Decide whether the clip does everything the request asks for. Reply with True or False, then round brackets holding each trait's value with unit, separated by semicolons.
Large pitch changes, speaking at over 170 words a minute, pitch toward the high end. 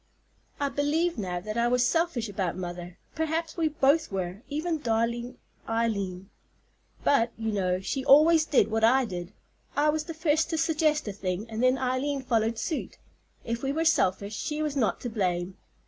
True (6.9 semitones; 180 wpm; 245 Hz)